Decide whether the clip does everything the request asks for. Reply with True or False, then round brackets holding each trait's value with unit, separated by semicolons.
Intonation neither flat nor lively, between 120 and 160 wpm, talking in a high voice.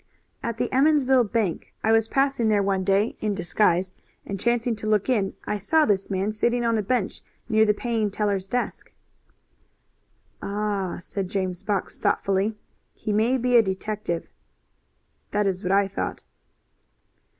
True (3.1 semitones; 155 wpm; 210 Hz)